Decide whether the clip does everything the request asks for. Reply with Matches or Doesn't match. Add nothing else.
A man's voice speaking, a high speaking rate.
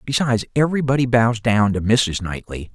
Doesn't match